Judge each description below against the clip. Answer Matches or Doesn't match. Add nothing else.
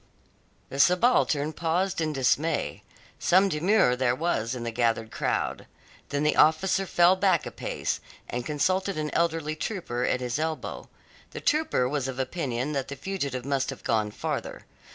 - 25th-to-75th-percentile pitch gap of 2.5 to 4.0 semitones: Doesn't match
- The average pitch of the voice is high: Doesn't match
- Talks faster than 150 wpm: Matches